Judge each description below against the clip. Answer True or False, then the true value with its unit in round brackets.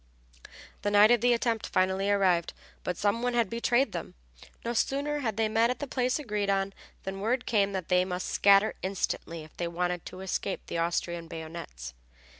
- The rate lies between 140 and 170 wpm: False (190 wpm)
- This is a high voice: True (200 Hz)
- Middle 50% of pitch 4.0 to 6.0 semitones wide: True (4.5 semitones)